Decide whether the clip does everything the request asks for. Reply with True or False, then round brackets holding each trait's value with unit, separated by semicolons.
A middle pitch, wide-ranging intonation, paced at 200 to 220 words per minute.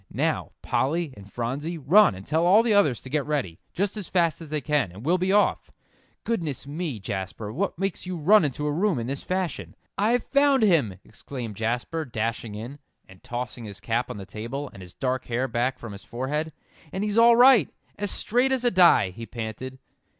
True (145 Hz; 8.1 semitones; 205 wpm)